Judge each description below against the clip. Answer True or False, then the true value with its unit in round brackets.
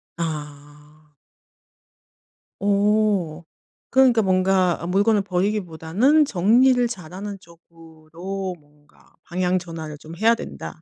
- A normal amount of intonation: True (4.2 semitones)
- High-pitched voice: False (180 Hz)